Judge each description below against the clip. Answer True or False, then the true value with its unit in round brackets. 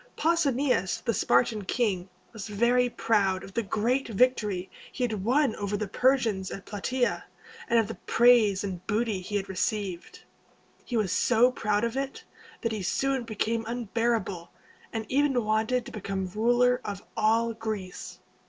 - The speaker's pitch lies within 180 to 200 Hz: False (220 Hz)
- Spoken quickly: False (155 wpm)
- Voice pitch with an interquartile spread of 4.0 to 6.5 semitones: False (3.5 semitones)